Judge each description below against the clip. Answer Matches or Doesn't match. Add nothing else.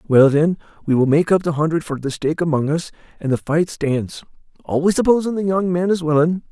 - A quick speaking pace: Matches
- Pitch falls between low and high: Matches